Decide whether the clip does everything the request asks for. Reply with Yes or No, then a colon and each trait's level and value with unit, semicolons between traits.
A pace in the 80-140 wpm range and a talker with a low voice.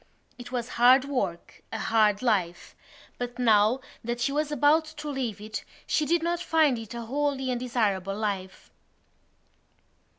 No: slow, 135 wpm; high, 245 Hz